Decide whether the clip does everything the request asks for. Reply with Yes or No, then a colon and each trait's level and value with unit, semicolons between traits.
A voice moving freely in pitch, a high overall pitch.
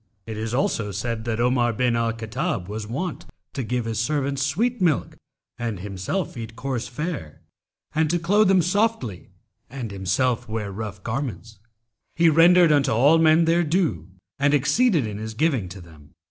No: wide, 6.6 semitones; low, 125 Hz